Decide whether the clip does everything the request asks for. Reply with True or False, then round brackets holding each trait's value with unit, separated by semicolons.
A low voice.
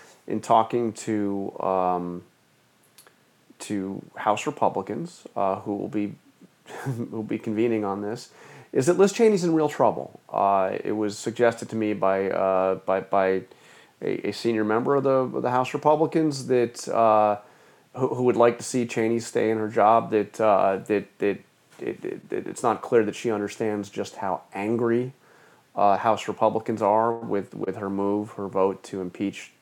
True (110 Hz)